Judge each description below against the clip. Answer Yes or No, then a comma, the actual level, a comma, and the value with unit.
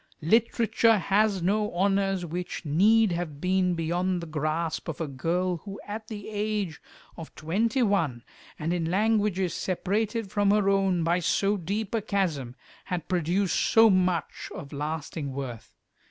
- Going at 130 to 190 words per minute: Yes, average, 150 wpm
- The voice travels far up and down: No, average, 3.9 semitones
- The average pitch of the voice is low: No, medium, 185 Hz